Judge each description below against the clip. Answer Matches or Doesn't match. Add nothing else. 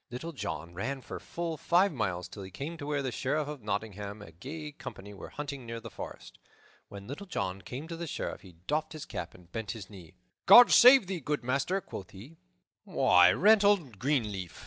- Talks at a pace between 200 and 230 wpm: Matches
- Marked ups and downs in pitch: Matches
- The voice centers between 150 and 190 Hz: Doesn't match